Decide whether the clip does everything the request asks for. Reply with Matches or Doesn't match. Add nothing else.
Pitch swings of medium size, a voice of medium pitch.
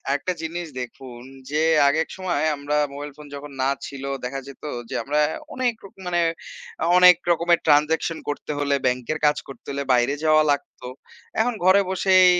Matches